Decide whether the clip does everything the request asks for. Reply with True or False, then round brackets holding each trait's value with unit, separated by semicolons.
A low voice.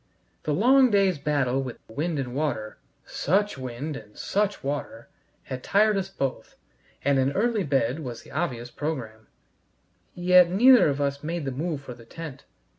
False (145 Hz)